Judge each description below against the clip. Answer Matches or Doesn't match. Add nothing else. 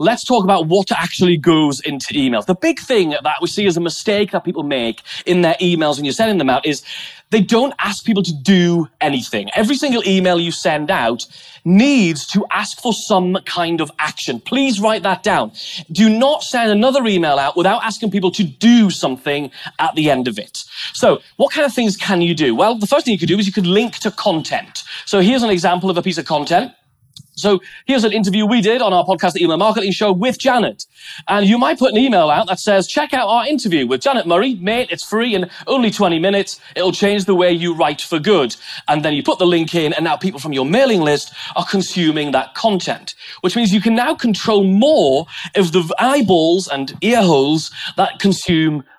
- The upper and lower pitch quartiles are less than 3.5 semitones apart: Doesn't match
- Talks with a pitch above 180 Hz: Matches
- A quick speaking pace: Matches